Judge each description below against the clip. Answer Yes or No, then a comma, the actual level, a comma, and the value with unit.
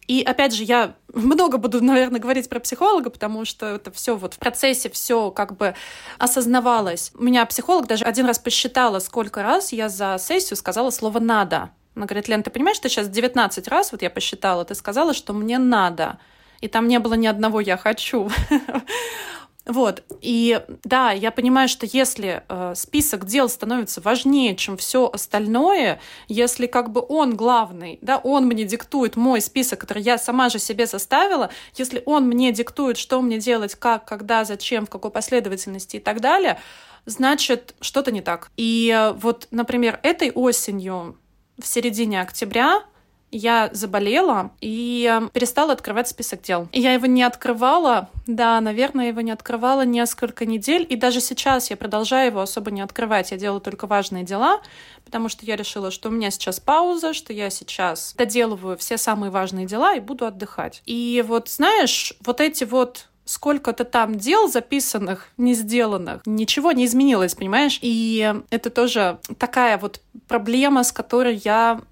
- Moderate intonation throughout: Yes, average, 3.0 semitones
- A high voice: Yes, high, 235 Hz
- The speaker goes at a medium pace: No, fast, 165 wpm